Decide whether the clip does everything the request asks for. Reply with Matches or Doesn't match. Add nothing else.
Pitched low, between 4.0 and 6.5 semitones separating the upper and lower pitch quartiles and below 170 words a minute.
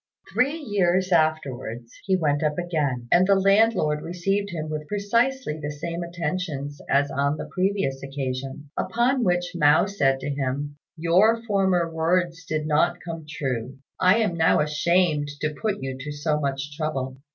Doesn't match